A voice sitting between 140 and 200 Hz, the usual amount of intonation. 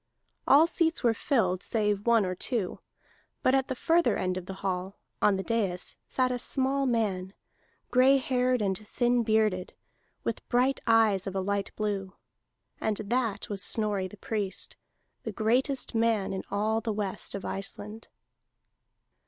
No: high, 215 Hz; average, 4.1 semitones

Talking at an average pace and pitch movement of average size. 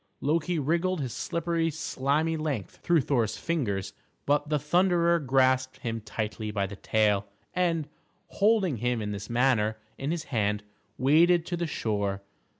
No: average, 150 wpm; wide, 7.3 semitones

